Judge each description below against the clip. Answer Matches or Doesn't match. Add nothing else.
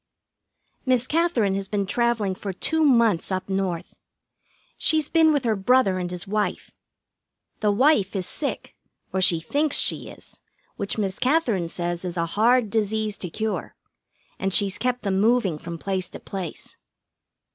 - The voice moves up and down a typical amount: Matches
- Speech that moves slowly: Doesn't match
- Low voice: Doesn't match